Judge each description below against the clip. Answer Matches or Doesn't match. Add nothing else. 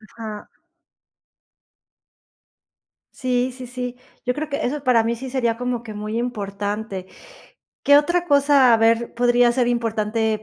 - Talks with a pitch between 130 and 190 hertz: Doesn't match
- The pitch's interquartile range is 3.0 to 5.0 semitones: Doesn't match